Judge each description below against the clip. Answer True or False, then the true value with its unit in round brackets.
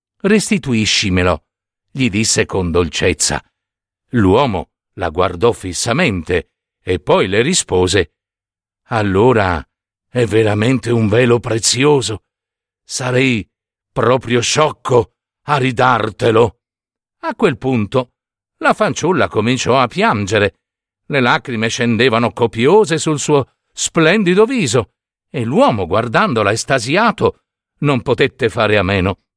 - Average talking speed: False (100 wpm)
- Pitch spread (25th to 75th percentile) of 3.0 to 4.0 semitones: False (4.4 semitones)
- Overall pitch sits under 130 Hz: True (115 Hz)